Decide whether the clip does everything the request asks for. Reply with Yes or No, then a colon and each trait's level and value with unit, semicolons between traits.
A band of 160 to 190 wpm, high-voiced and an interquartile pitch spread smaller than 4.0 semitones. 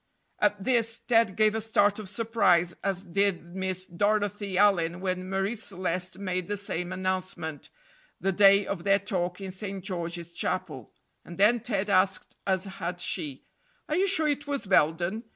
Yes: average, 165 wpm; high, 195 Hz; narrow, 2.4 semitones